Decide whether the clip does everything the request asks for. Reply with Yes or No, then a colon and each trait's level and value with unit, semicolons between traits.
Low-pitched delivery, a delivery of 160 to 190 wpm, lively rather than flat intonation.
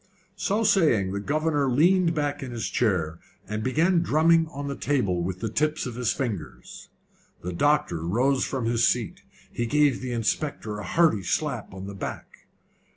Yes: low, 130 Hz; average, 170 wpm; wide, 6.6 semitones